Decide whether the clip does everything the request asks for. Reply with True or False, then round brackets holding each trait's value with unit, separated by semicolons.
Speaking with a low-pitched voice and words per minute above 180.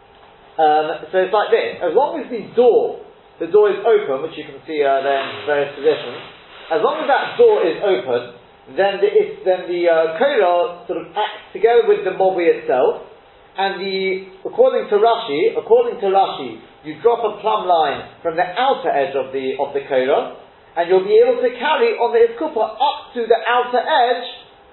False (235 Hz; 190 wpm)